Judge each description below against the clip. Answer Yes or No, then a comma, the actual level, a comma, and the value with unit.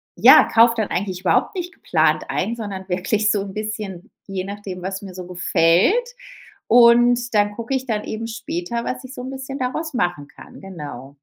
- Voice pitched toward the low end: No, high, 210 Hz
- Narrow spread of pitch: No, average, 4.4 semitones